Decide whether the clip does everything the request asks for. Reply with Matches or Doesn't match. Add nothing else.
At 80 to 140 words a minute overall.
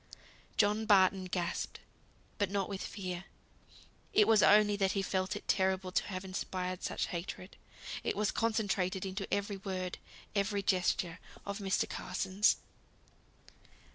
Matches